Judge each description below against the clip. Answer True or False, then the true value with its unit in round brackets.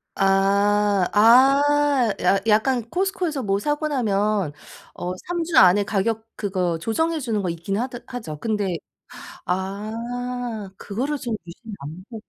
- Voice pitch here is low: False (215 Hz)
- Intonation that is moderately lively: True (4.7 semitones)